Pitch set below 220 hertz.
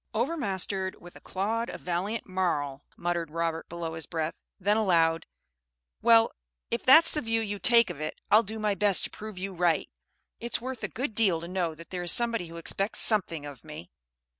Yes: high, 190 Hz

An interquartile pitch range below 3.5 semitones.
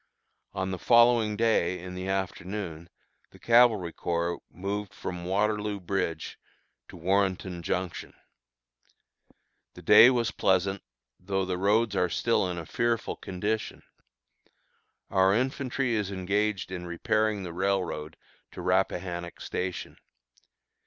Yes: average, 3.0 semitones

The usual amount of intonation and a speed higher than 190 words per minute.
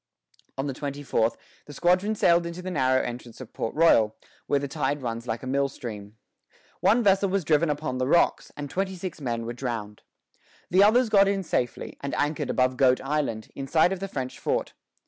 No: wide, 5.7 semitones; fast, 205 wpm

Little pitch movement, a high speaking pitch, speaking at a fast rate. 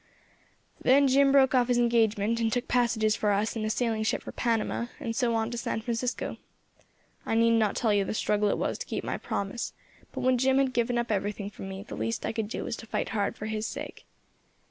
Yes: narrow, 2.2 semitones; high, 230 Hz; fast, 235 wpm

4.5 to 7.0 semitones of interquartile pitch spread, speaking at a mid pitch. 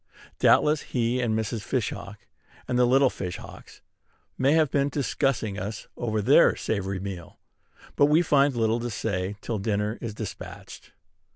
No: average, 4.8 semitones; low, 115 Hz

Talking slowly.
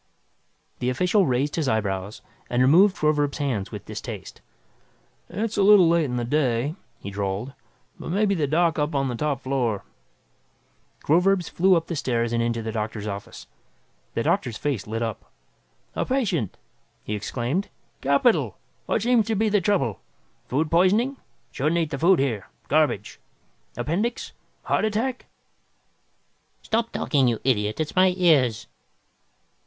No: average, 150 wpm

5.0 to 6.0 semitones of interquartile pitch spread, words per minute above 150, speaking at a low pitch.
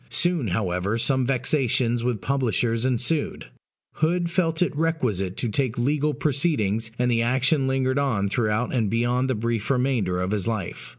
No: average, 3.8 semitones; average, 160 wpm; low, 125 Hz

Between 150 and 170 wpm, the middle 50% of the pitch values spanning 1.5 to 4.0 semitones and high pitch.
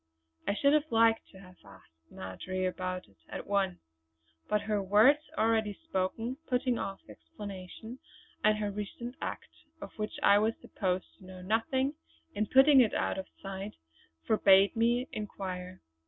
Yes: average, 155 wpm; average, 3.4 semitones; high, 205 Hz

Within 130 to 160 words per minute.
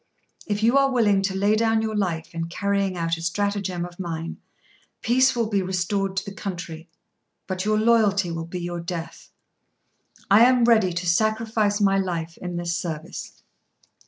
No: average, 170 wpm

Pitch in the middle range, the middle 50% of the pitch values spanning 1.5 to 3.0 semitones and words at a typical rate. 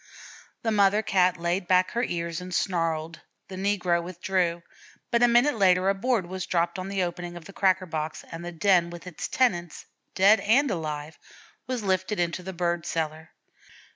Yes: medium, 180 Hz; narrow, 2.5 semitones; average, 180 wpm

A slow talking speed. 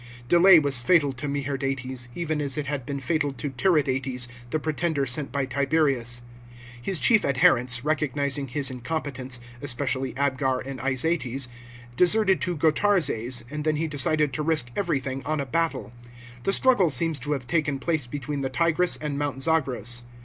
No: average, 165 wpm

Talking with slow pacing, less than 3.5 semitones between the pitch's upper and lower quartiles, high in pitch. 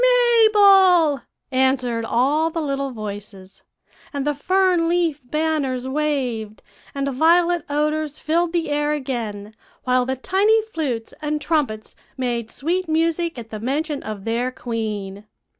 No: slow, 130 wpm; wide, 5.5 semitones; very high, 285 Hz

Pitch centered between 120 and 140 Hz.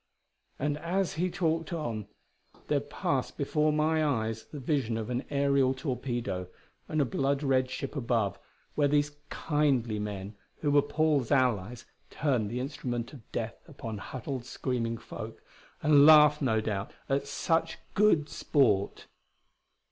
Yes: low, 135 Hz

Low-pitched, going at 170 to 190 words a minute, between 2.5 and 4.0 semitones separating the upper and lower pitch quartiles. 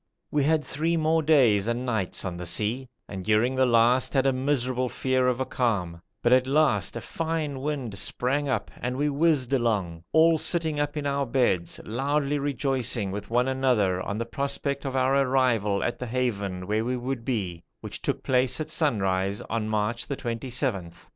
No: low, 125 Hz; average, 185 wpm; average, 4.4 semitones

